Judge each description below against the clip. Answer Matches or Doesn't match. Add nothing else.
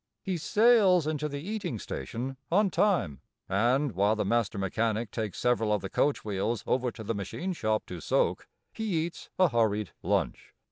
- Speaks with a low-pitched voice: Matches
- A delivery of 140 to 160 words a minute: Doesn't match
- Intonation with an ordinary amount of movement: Doesn't match